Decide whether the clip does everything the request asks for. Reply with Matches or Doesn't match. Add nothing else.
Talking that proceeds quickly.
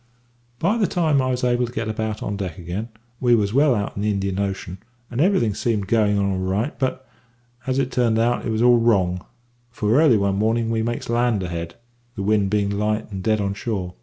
Matches